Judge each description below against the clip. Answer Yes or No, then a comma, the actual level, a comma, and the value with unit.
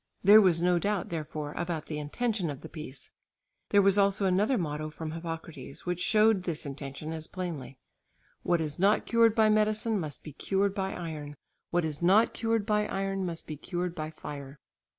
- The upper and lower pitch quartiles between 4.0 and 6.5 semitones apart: Yes, average, 4.6 semitones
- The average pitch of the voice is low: No, medium, 175 Hz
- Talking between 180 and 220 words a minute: Yes, average, 185 wpm